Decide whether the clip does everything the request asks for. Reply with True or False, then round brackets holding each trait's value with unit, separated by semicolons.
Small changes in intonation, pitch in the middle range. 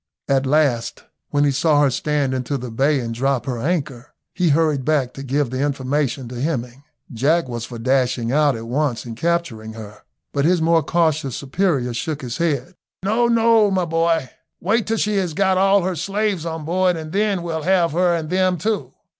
False (5.0 semitones; 150 Hz)